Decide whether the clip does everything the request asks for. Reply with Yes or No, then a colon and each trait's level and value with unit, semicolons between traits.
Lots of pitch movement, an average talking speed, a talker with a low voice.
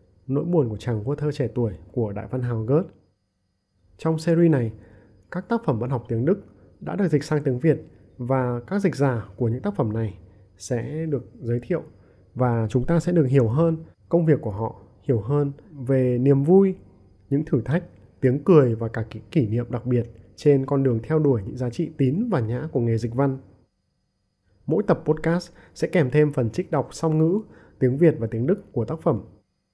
Yes: wide, 5.8 semitones; average, 210 wpm; low, 130 Hz